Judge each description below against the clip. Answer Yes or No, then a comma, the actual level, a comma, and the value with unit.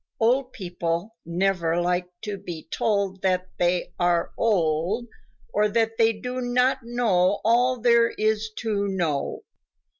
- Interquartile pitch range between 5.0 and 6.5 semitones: No, average, 4.6 semitones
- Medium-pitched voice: No, high, 205 Hz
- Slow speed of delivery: Yes, slow, 130 wpm